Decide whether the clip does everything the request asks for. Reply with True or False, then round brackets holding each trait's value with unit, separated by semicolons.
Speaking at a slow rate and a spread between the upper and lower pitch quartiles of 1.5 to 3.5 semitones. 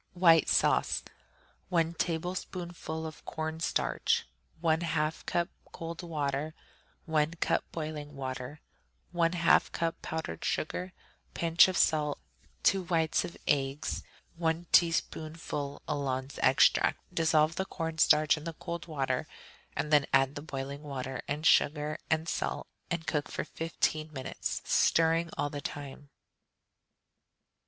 True (125 wpm; 2.4 semitones)